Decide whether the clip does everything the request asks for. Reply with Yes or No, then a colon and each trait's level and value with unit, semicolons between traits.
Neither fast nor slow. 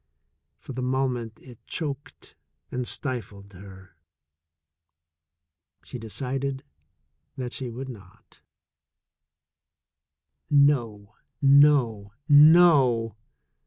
No: slow, 80 wpm